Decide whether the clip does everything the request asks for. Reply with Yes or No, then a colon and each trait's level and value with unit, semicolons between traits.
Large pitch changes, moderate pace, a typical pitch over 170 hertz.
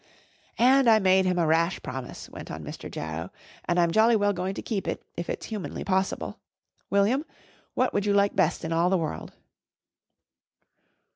No: average, 3.6 semitones; average, 180 wpm; high, 190 Hz